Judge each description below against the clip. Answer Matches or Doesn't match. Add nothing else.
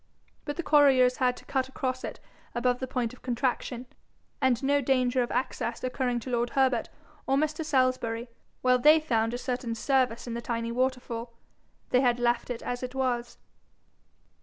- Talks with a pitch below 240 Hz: Doesn't match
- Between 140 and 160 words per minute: Doesn't match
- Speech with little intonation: Matches